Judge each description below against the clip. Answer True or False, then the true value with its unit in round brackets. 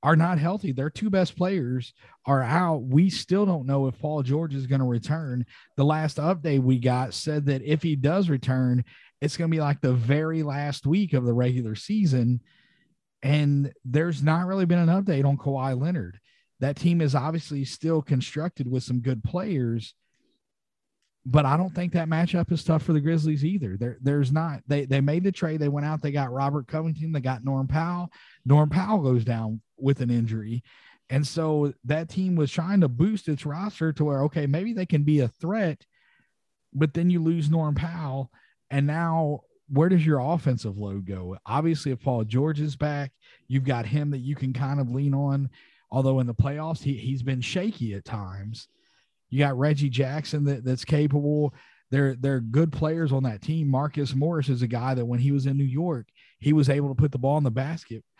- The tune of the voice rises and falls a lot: False (3.4 semitones)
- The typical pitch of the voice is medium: True (145 Hz)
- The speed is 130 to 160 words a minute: False (205 wpm)